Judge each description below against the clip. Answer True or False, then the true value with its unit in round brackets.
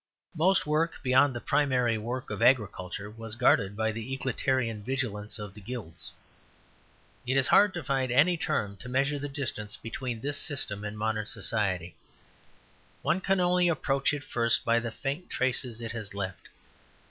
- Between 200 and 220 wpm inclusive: False (165 wpm)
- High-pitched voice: False (120 Hz)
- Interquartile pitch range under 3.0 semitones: False (4.3 semitones)